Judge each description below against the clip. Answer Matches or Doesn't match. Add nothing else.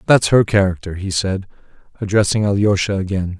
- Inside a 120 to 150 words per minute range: Matches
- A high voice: Doesn't match